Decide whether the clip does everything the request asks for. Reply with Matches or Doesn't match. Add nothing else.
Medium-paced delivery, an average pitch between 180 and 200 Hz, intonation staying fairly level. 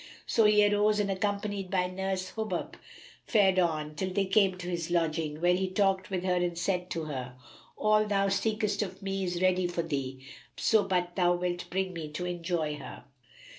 Matches